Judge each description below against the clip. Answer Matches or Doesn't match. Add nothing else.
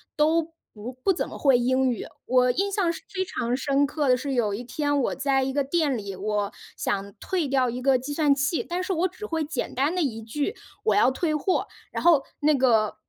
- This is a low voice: Doesn't match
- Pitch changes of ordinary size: Matches